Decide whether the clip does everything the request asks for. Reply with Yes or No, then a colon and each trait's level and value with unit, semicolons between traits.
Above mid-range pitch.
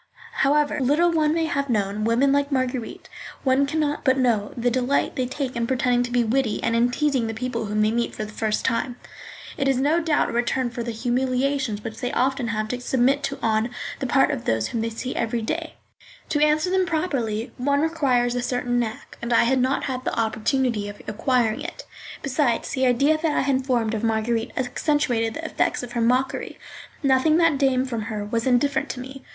Yes: very high, 250 Hz